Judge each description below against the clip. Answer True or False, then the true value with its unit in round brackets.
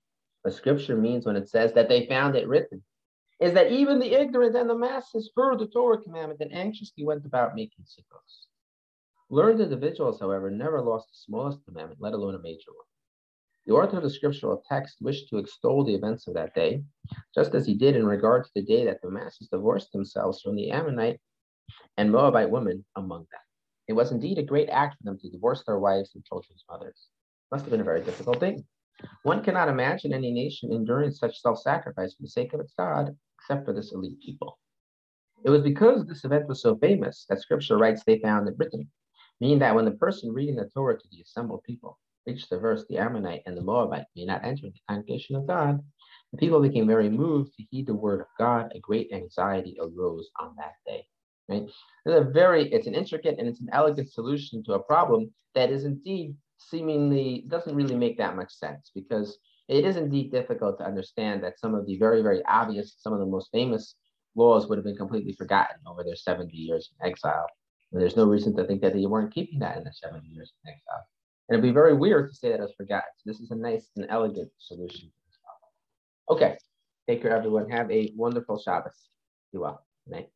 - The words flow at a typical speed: False (210 wpm)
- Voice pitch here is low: True (125 Hz)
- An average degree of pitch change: False (6.3 semitones)